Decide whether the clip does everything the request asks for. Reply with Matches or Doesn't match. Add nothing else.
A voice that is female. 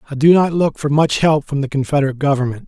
Doesn't match